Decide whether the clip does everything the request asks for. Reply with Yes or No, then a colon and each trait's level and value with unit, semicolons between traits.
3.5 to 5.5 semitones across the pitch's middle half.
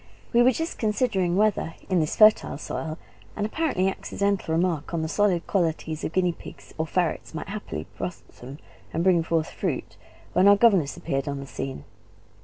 Yes: average, 4.3 semitones